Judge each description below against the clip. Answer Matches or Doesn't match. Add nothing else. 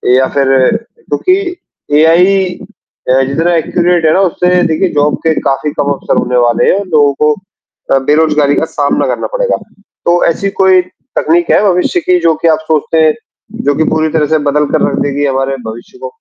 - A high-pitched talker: Doesn't match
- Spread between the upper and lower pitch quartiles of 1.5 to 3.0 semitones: Doesn't match